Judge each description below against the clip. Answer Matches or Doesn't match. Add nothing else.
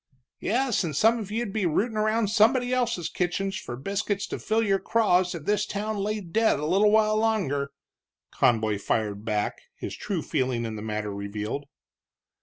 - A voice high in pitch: Matches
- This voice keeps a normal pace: Matches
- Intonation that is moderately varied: Doesn't match